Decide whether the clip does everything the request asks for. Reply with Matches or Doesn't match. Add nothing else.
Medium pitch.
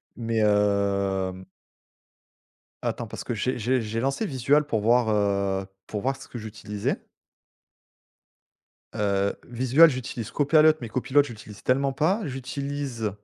Doesn't match